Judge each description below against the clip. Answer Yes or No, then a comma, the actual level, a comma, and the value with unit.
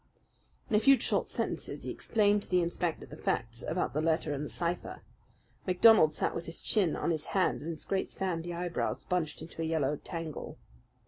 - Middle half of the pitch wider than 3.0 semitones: No, average, 2.7 semitones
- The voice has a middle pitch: Yes, medium, 170 Hz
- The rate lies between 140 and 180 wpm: No, average, 195 wpm